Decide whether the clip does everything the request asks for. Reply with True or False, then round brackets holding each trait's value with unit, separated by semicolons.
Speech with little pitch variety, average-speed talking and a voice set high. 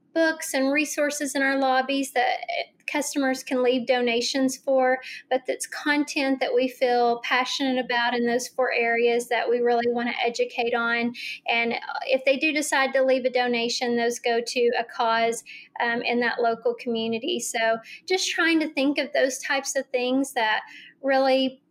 True (2.2 semitones; 170 wpm; 255 Hz)